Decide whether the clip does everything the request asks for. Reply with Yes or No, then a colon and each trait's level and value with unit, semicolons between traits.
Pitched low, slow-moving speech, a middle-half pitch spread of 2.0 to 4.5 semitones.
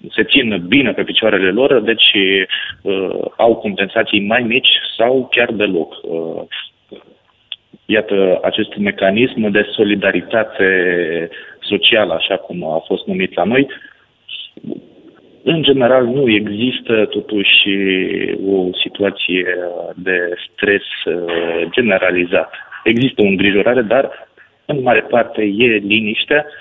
Yes: low, 105 Hz; slow, 110 wpm; average, 3.1 semitones